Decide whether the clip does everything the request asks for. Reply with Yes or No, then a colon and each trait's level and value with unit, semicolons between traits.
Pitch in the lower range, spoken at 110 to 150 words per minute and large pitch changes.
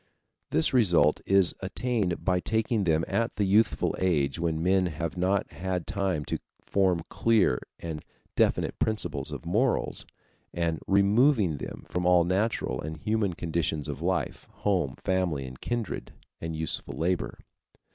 No: very low, 90 Hz; average, 145 wpm; average, 3.7 semitones